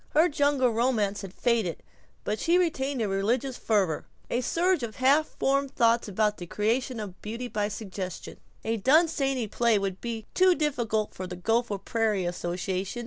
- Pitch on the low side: No, high, 230 Hz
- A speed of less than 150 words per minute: No, average, 165 wpm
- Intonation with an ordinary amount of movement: Yes, average, 4.7 semitones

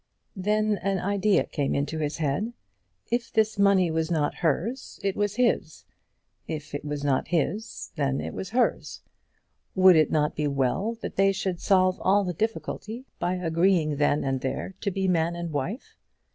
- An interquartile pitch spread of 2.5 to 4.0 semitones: No, average, 5.0 semitones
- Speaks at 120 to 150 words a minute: No, average, 170 wpm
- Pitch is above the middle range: No, medium, 180 Hz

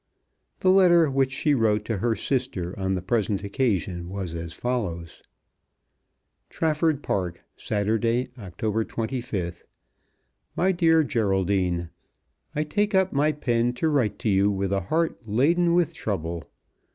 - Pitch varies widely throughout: Yes, wide, 7.3 semitones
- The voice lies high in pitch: No, low, 115 Hz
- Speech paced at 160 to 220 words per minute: No, slow, 135 wpm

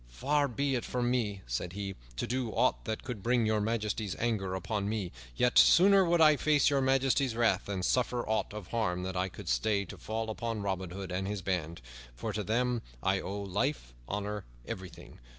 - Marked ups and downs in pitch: No, average, 4.5 semitones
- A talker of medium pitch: No, low, 110 Hz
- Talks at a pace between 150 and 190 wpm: No, average, 200 wpm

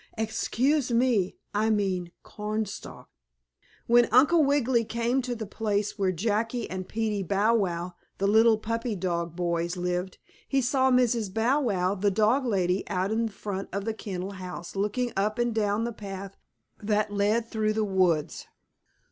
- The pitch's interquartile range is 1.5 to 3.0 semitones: No, average, 3.4 semitones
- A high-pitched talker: Yes, high, 210 Hz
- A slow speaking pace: No, average, 160 wpm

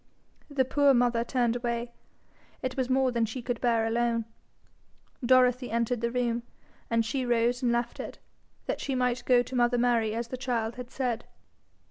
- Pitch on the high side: Yes, high, 240 Hz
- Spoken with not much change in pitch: Yes, narrow, 1.2 semitones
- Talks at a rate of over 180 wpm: No, average, 175 wpm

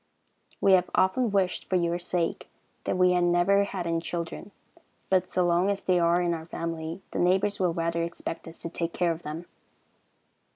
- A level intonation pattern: Yes, narrow, 1.7 semitones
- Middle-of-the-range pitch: Yes, medium, 175 Hz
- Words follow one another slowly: No, average, 195 wpm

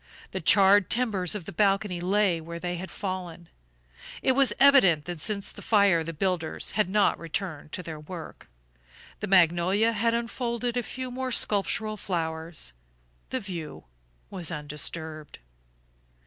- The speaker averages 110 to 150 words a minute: Yes, average, 145 wpm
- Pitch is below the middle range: No, high, 190 Hz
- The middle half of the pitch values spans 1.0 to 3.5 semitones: No, average, 4.2 semitones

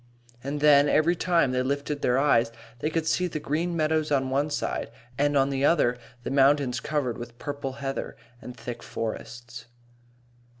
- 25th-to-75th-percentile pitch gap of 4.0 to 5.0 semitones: No, average, 3.0 semitones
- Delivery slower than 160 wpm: No, average, 170 wpm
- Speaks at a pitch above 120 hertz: Yes, medium, 140 Hz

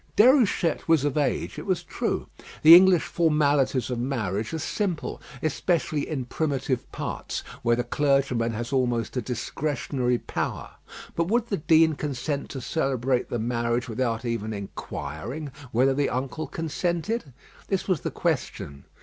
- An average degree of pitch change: Yes, average, 4.8 semitones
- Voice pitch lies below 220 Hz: Yes, low, 135 Hz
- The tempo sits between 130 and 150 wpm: Yes, average, 145 wpm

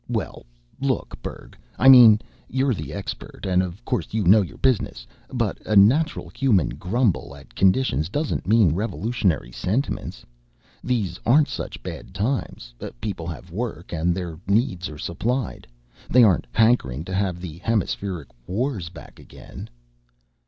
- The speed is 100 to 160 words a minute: Yes, average, 145 wpm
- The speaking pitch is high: No, low, 100 Hz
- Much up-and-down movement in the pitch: Yes, wide, 5.9 semitones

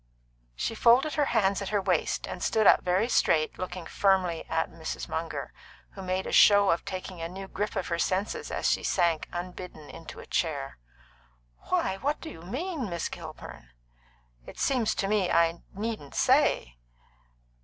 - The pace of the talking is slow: No, average, 175 wpm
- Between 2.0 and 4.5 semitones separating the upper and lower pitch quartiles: Yes, average, 3.8 semitones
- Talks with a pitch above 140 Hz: Yes, medium, 185 Hz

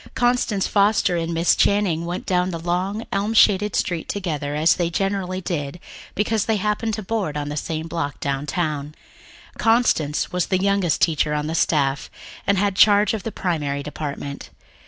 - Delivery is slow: No, average, 170 wpm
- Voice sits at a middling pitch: Yes, medium, 175 Hz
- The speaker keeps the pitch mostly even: No, average, 4.8 semitones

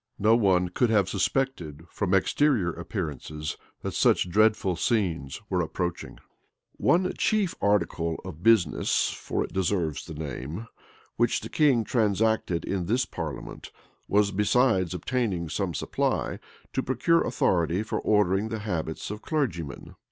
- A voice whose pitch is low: Yes, very low, 95 Hz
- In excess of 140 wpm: No, slow, 135 wpm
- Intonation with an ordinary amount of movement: Yes, average, 4.9 semitones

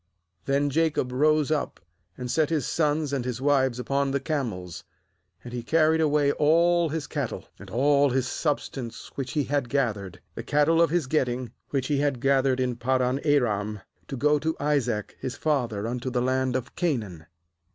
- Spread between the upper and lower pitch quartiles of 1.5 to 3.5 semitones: Yes, average, 3.2 semitones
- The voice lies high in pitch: No, low, 135 Hz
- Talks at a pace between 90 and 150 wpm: No, average, 175 wpm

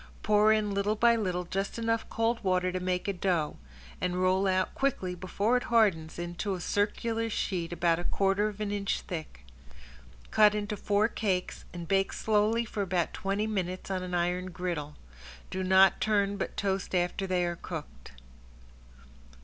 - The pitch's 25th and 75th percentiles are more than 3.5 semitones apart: No, average, 2.7 semitones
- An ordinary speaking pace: Yes, average, 170 wpm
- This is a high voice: Yes, high, 195 Hz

